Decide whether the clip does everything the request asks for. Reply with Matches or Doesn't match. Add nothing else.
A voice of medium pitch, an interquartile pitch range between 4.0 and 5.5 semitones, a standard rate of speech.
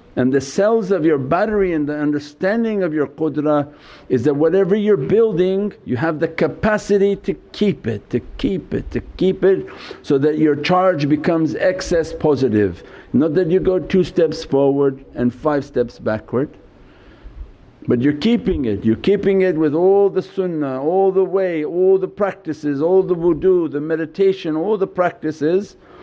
Matches